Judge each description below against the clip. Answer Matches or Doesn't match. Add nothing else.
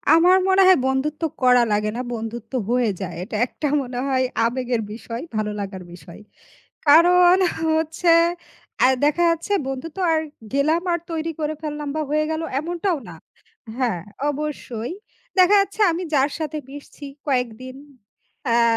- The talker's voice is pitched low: Doesn't match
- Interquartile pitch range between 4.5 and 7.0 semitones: Matches